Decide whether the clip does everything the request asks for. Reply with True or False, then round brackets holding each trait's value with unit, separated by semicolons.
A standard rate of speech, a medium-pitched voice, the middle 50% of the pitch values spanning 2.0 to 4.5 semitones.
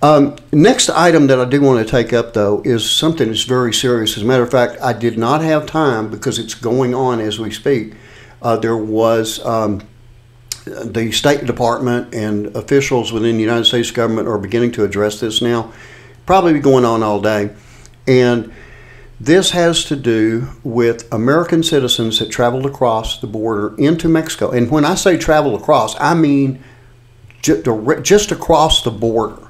False (175 wpm; 120 Hz; 3.6 semitones)